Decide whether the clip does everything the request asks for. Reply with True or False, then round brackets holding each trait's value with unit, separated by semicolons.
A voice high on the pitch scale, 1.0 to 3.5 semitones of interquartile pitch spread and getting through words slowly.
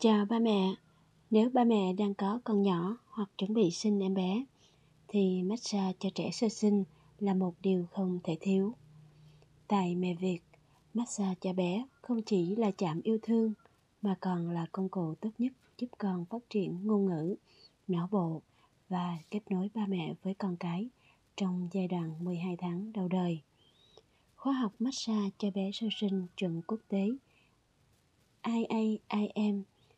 True (195 Hz; 3.1 semitones; 160 wpm)